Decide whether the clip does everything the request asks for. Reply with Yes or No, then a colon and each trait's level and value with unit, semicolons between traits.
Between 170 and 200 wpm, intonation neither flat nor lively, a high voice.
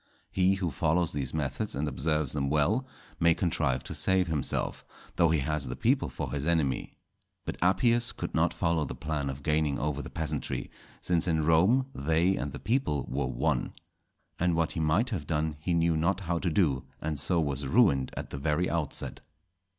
No: average, 190 wpm; average, 3.5 semitones; very low, 80 Hz